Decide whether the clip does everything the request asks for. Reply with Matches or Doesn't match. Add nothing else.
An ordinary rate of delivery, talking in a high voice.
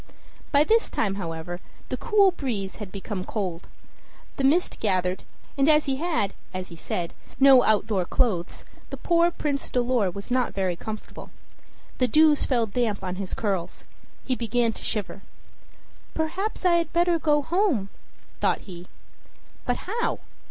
Matches